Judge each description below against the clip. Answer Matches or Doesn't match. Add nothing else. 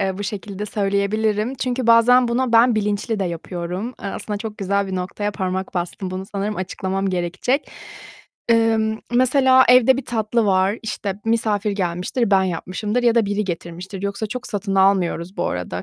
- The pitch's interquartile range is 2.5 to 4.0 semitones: Matches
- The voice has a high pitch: Matches